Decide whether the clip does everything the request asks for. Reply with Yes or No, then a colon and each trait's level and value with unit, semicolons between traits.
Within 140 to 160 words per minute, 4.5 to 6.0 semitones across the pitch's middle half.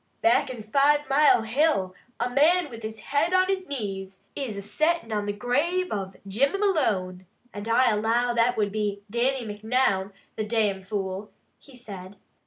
No: average, 170 wpm; wide, 5.6 semitones